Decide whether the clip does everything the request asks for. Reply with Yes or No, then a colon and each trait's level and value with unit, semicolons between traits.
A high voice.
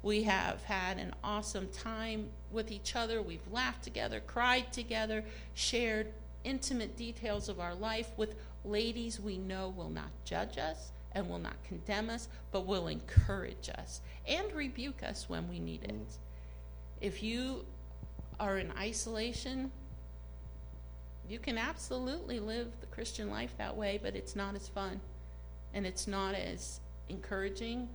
Yes: high, 200 Hz